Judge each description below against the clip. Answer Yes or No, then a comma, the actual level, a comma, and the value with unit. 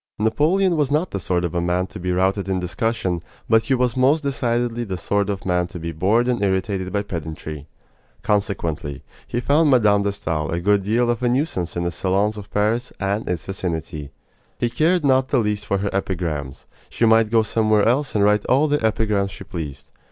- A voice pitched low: Yes, low, 100 Hz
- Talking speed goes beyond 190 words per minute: Yes, fast, 205 wpm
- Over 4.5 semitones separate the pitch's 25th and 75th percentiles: Yes, average, 4.9 semitones